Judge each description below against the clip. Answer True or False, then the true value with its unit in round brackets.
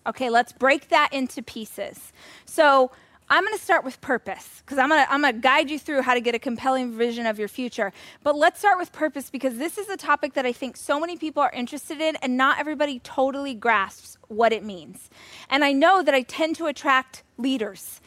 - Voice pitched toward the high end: True (270 Hz)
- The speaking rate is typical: False (215 wpm)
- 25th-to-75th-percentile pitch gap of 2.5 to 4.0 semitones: True (3.7 semitones)